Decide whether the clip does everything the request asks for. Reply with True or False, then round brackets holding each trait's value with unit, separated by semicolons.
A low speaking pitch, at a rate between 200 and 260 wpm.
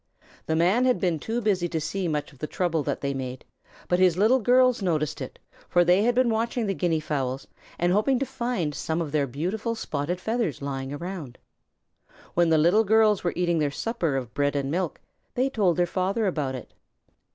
False (175 Hz; 205 wpm)